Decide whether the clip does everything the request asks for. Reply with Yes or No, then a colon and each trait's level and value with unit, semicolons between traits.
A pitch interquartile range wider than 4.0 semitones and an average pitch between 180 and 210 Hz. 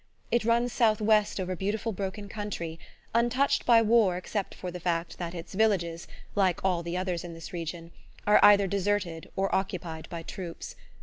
No: average, 3.7 semitones; high, 190 Hz